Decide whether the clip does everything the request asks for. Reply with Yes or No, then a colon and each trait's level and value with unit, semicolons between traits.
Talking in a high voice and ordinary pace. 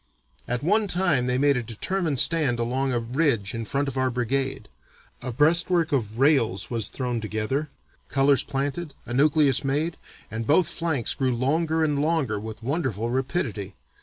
No: low, 135 Hz; average, 165 wpm